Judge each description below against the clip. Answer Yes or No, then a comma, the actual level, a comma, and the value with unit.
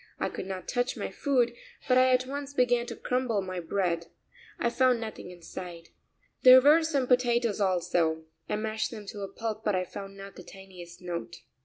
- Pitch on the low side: No, high, 215 Hz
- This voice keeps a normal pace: Yes, average, 190 wpm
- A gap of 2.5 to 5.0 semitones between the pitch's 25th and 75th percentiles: No, wide, 5.4 semitones